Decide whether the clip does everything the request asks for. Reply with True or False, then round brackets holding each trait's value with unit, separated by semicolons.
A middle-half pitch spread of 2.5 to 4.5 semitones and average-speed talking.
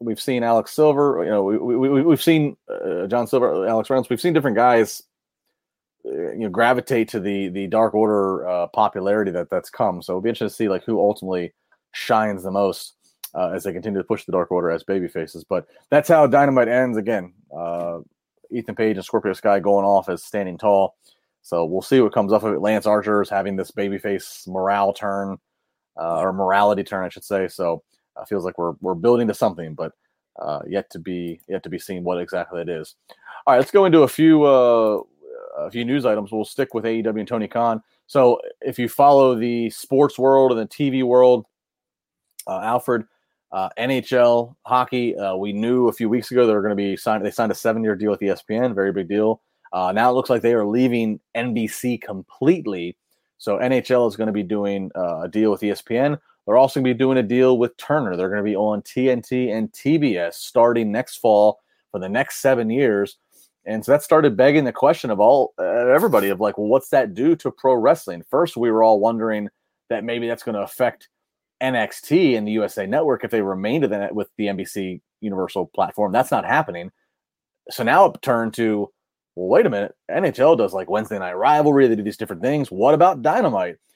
False (4.0 semitones; 210 wpm)